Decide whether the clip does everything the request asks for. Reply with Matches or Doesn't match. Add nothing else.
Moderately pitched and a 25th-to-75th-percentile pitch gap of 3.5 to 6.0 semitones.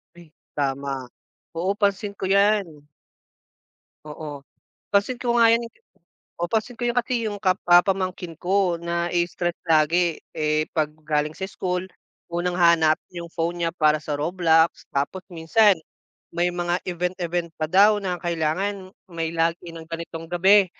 Doesn't match